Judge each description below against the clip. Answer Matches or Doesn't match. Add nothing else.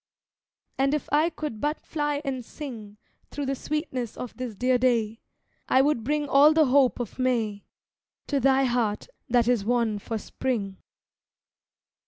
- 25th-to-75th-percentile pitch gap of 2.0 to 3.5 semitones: Doesn't match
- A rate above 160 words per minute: Doesn't match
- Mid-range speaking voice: Doesn't match